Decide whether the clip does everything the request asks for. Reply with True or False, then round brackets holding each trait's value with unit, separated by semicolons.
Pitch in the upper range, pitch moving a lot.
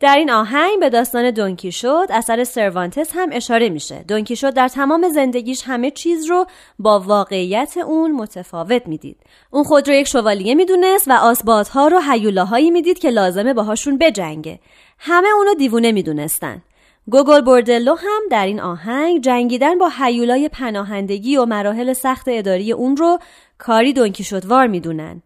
True (250 Hz; 5.8 semitones)